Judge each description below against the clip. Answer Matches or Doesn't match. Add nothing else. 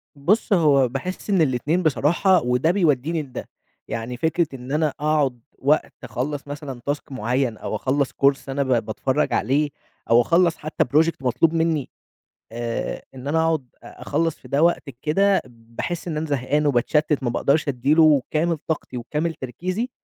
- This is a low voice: Doesn't match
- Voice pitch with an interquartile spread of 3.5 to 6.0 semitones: Matches